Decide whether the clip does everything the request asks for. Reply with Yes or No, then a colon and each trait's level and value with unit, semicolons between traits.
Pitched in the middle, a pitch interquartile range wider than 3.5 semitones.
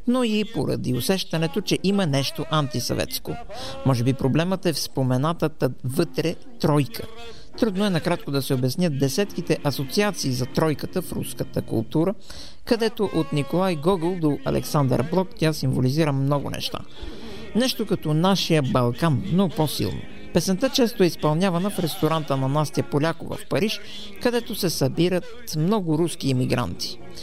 Yes: medium, 160 Hz; wide, 5.6 semitones